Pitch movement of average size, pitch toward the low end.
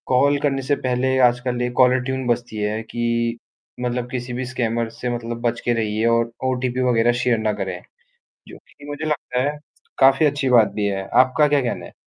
No: narrow, 2.0 semitones; low, 125 Hz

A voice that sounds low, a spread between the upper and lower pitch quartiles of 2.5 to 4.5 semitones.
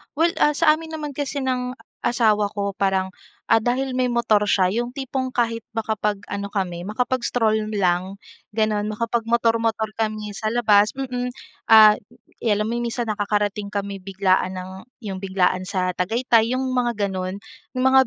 No: high, 220 Hz; average, 3.5 semitones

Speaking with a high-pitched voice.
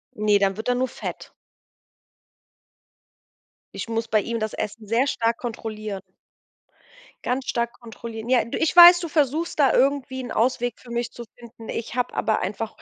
Yes: high, 235 Hz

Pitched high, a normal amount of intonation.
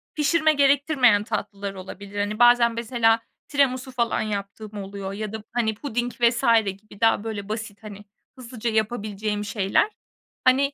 Yes: high, 220 Hz; average, 3.1 semitones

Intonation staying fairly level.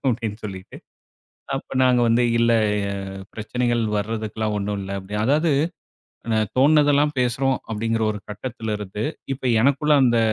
No: average, 3.7 semitones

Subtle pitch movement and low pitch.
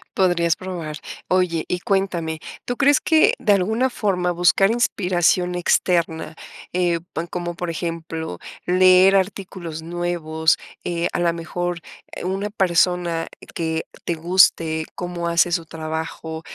No: narrow, 2.0 semitones; medium, 175 Hz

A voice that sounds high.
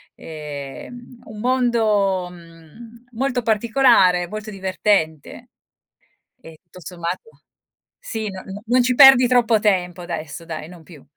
Yes: high, 200 Hz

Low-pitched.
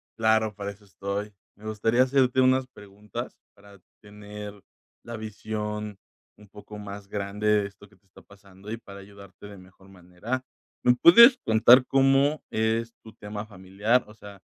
Yes: low, 105 Hz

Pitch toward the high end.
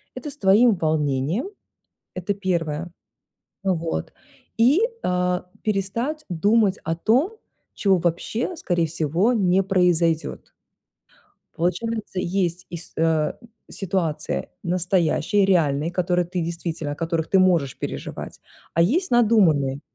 No: medium, 180 Hz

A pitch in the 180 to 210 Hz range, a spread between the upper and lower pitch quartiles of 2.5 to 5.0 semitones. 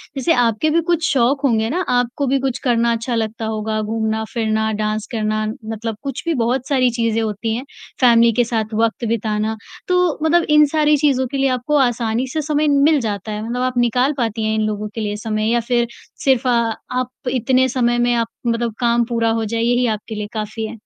No: high, 235 Hz; average, 2.9 semitones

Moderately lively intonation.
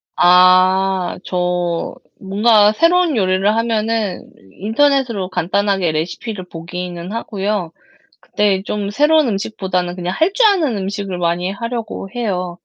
Yes: average, 3.9 semitones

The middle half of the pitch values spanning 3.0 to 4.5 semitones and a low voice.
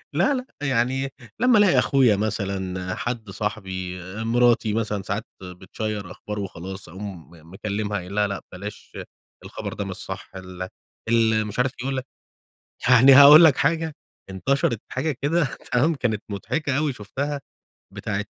No: wide, 5.4 semitones; low, 110 Hz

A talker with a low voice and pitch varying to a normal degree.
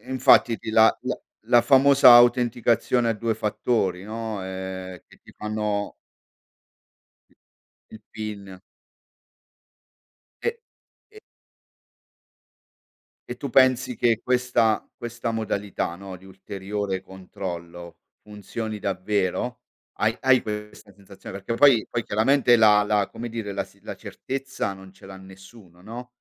Yes: low, 105 Hz; average, 3.7 semitones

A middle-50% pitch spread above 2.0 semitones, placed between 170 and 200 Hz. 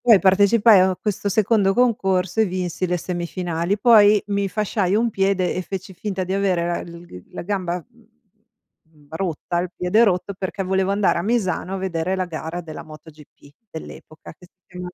Yes: narrow, 2.6 semitones; medium, 185 Hz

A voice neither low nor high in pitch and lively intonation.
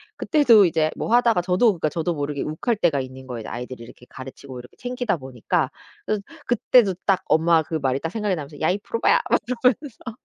Yes: medium, 170 Hz; wide, 8.3 semitones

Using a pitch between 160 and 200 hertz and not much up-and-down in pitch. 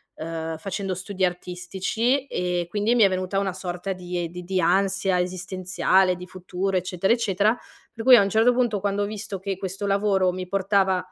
Yes: high, 190 Hz; narrow, 1.9 semitones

